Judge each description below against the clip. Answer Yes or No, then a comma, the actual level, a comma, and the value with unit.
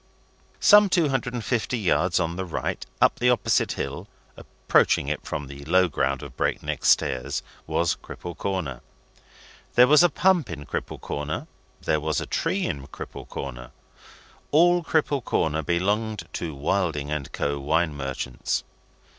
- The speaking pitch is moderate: No, very low, 85 Hz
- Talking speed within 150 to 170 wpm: Yes, average, 155 wpm